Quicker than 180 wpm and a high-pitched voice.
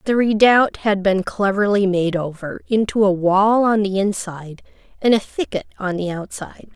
No: average, 170 wpm; high, 200 Hz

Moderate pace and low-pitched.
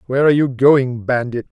Yes: average, 190 wpm; low, 130 Hz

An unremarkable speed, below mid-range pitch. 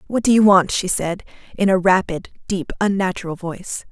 No: average, 185 wpm; high, 190 Hz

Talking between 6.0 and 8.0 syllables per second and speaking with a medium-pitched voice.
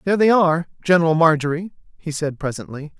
Yes: 6.5 syllables/s; medium, 165 Hz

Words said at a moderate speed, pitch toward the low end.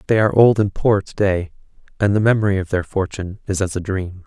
No: fast, 240 wpm; very low, 95 Hz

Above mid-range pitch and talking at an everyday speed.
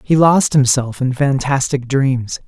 No: low, 135 Hz; average, 145 wpm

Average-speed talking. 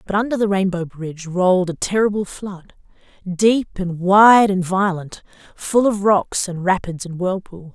Yes: average, 165 wpm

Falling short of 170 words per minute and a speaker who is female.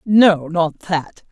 Yes: slow, 135 wpm; female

